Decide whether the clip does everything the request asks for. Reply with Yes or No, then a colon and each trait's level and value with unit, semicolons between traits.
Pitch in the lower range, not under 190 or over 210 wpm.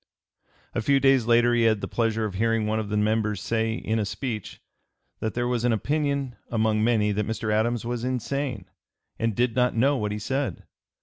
Yes: low, 115 Hz; average, 200 wpm